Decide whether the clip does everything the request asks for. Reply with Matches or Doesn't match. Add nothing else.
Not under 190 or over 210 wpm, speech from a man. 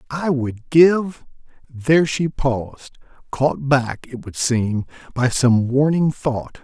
Doesn't match